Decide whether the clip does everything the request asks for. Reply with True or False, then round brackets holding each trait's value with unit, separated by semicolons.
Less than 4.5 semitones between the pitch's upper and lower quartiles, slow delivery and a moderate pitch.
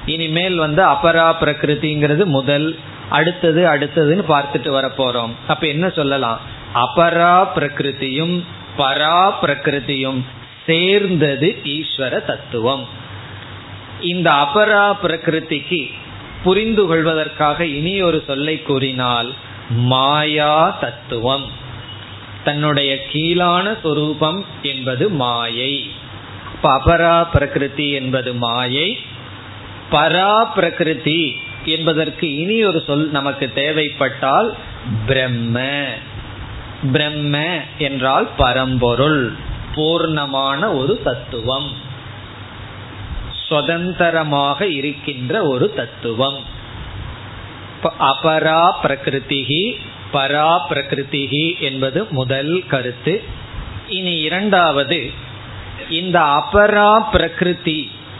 False (4.8 semitones; 70 wpm; 145 Hz)